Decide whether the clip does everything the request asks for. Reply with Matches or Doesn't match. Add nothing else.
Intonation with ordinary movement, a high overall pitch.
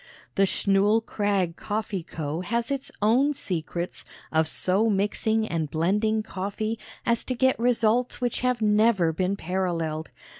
Matches